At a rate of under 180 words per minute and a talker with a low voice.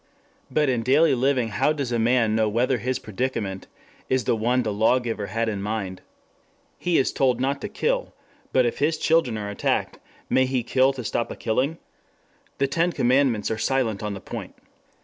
No: average, 190 wpm; low, 125 Hz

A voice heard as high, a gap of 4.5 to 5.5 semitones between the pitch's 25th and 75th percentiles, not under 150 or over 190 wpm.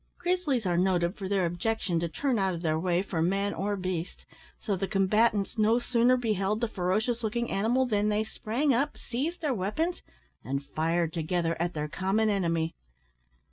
Yes: high, 200 Hz; average, 4.9 semitones; average, 180 wpm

